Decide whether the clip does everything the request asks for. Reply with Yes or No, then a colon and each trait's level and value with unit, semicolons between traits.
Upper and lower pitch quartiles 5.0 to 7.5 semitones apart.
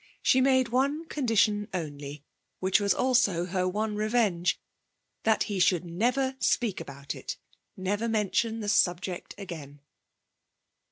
No: average, 4.6 semitones